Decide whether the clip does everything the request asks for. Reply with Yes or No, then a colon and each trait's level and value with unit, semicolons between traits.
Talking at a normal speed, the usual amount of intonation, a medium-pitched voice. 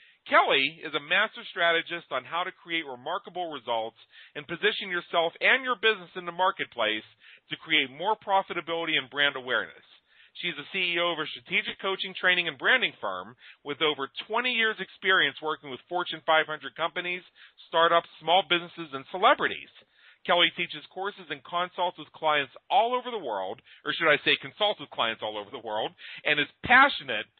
Yes: average, 170 wpm; average, 3.8 semitones; medium, 170 Hz